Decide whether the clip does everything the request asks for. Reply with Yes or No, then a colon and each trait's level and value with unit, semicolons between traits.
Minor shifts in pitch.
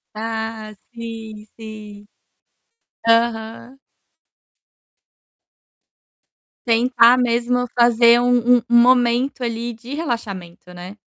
Yes: narrow, 1.7 semitones